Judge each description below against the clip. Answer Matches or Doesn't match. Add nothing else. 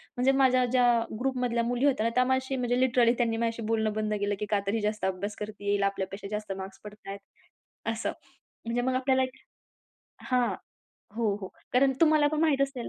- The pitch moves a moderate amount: Matches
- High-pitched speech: Matches